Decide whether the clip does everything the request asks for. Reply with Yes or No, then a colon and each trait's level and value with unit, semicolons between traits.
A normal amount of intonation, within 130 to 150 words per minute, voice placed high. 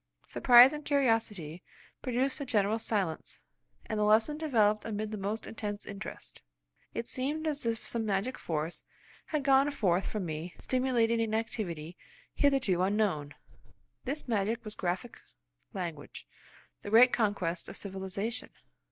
Yes: average, 4.6 semitones; slow, 135 wpm; high, 215 Hz